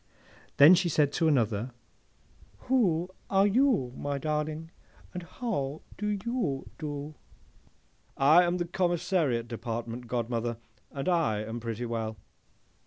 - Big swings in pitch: Yes, wide, 6.9 semitones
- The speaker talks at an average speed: No, slow, 115 wpm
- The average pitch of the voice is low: No, medium, 150 Hz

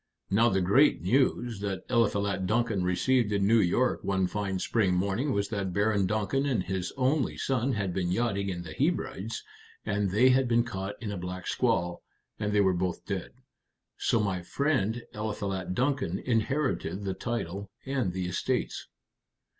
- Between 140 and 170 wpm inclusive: Yes, average, 165 wpm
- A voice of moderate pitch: No, low, 100 Hz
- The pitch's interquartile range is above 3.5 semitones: Yes, average, 4.0 semitones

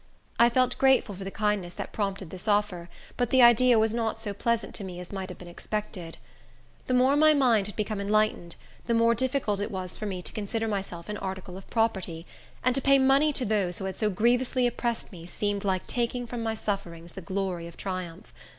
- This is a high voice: Yes, high, 210 Hz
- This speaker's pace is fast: Yes, fast, 215 wpm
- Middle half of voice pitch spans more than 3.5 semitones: Yes, average, 4.0 semitones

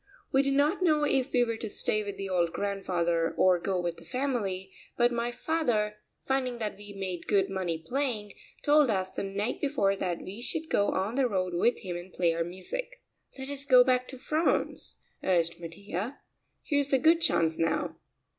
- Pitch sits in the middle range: No, high, 210 Hz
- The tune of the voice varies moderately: No, wide, 6.4 semitones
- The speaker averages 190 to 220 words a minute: Yes, average, 195 wpm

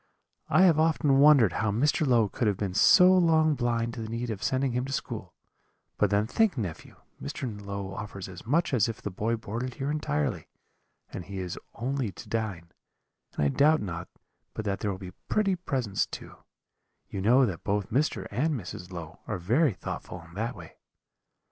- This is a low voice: Yes, low, 115 Hz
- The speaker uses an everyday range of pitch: No, wide, 5.7 semitones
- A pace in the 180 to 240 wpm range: Yes, average, 190 wpm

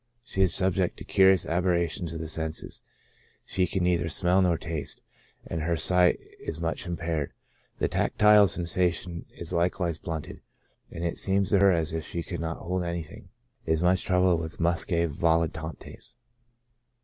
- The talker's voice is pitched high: No, very low, 85 Hz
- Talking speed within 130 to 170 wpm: Yes, average, 160 wpm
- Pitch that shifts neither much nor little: No, narrow, 1.9 semitones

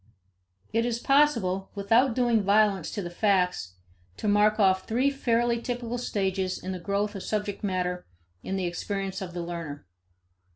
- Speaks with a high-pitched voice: Yes, high, 200 Hz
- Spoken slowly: No, average, 160 wpm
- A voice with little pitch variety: No, average, 3.7 semitones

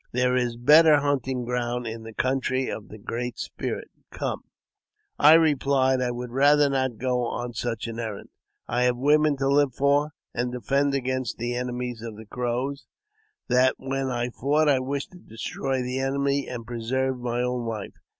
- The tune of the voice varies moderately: No, narrow, 2.3 semitones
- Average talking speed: Yes, average, 180 wpm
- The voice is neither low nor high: No, low, 125 Hz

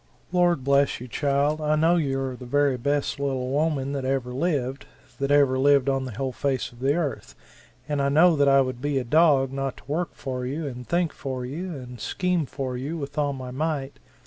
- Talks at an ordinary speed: No, fast, 220 wpm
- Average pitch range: No, narrow, 2.3 semitones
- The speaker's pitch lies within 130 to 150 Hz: Yes, medium, 140 Hz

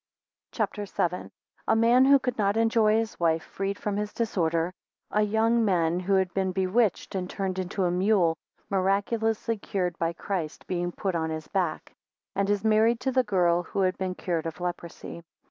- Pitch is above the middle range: Yes, high, 195 Hz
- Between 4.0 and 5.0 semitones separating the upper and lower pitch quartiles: No, average, 3.6 semitones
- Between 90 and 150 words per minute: No, average, 195 wpm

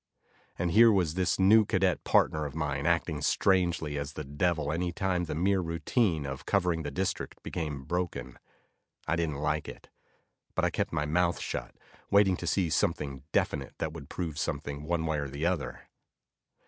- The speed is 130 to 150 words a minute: No, average, 175 wpm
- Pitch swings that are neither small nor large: Yes, average, 3.5 semitones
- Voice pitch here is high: No, very low, 80 Hz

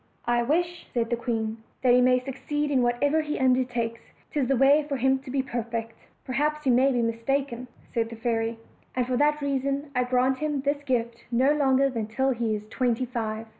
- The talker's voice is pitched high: Yes, very high, 255 Hz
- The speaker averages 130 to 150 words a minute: No, fast, 205 wpm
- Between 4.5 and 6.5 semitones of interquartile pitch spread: No, average, 2.9 semitones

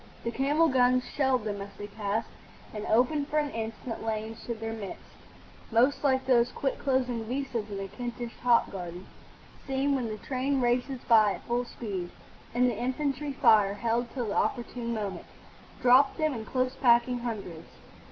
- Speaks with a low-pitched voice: No, high, 240 Hz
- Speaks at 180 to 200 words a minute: No, average, 170 wpm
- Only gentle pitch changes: No, average, 3.0 semitones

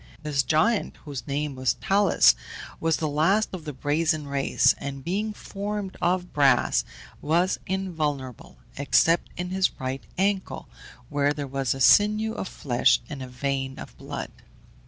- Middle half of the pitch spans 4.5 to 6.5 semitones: Yes, wide, 5.4 semitones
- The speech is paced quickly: No, average, 150 wpm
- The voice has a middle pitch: Yes, medium, 150 Hz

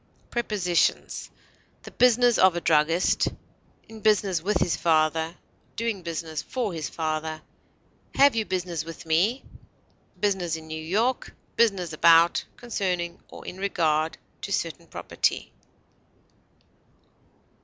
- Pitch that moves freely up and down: No, average, 4.6 semitones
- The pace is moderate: No, slow, 115 wpm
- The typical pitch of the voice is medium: Yes, medium, 175 Hz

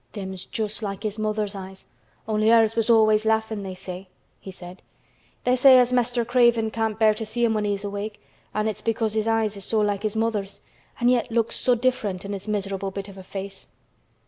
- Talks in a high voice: Yes, high, 215 Hz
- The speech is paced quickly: Yes, fast, 210 wpm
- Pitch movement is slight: Yes, narrow, 2.3 semitones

